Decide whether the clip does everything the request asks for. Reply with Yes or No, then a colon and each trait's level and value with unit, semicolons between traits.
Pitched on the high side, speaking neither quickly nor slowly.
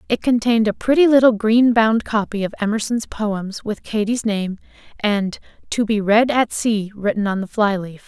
Yes: high, 215 Hz; average, 180 wpm